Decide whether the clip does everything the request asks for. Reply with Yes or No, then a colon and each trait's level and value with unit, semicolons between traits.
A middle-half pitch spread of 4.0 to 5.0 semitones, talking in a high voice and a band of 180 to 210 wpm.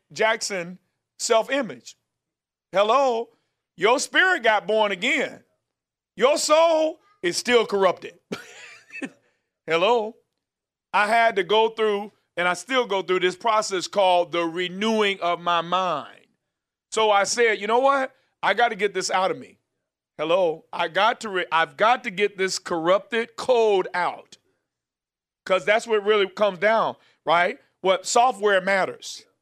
No: average, 4.4 semitones; high, 215 Hz; average, 145 wpm